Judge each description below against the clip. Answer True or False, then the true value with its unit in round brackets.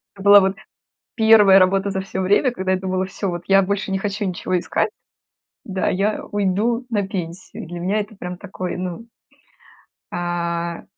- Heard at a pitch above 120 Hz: True (190 Hz)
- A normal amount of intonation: False (1.9 semitones)